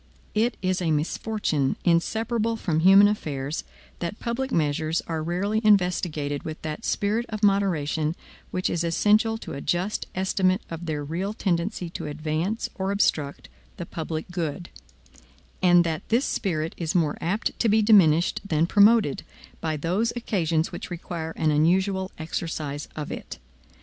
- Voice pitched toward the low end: No, medium, 175 Hz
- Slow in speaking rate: No, average, 150 wpm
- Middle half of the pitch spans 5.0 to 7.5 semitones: No, average, 4.5 semitones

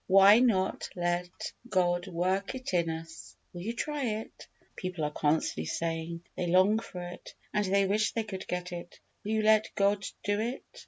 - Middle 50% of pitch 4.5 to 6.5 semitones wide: No, average, 3.3 semitones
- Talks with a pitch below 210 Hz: Yes, medium, 185 Hz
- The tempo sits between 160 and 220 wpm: Yes, average, 180 wpm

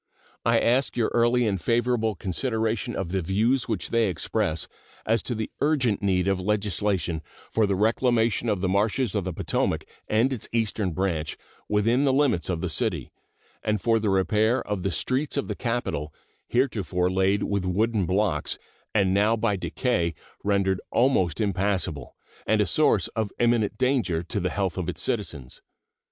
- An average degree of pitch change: Yes, average, 3.9 semitones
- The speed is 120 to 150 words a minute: No, average, 170 wpm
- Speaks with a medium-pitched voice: No, low, 105 Hz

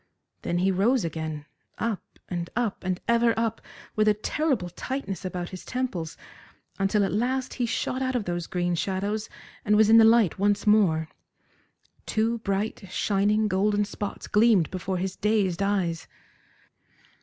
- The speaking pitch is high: Yes, high, 205 Hz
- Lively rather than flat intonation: No, average, 3.3 semitones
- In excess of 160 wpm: No, average, 155 wpm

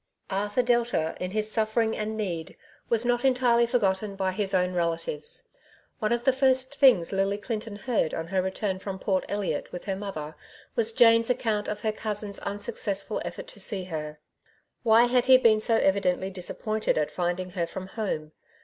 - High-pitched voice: Yes, high, 210 Hz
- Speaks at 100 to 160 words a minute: No, average, 175 wpm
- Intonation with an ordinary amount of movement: Yes, average, 3.7 semitones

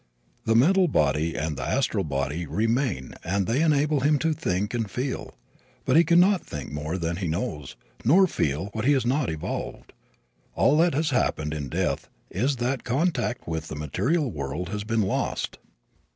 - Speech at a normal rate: Yes, average, 180 wpm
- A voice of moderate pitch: No, low, 110 Hz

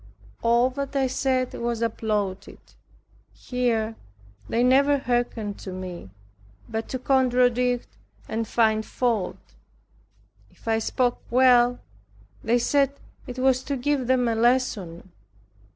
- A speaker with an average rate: No, slow, 120 wpm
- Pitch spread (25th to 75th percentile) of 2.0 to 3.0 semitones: Yes, narrow, 2.5 semitones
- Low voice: No, high, 245 Hz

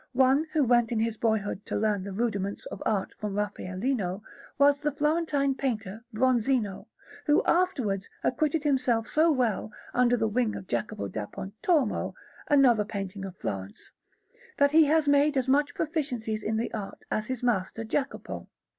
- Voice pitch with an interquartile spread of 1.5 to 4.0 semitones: No, wide, 5.4 semitones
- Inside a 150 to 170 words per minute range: Yes, average, 160 wpm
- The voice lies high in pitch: Yes, high, 235 Hz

